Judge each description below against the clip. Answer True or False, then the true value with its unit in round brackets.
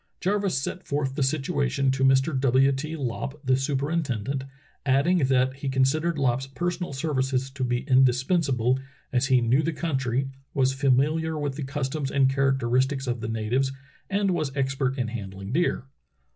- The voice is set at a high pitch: False (135 Hz)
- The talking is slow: False (170 wpm)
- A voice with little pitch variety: True (2.1 semitones)